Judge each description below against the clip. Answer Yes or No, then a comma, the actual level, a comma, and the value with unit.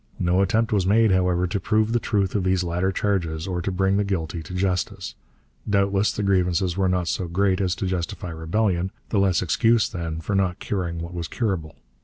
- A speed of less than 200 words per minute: No, fast, 205 wpm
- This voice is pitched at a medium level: No, very low, 95 Hz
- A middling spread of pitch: No, narrow, 2.2 semitones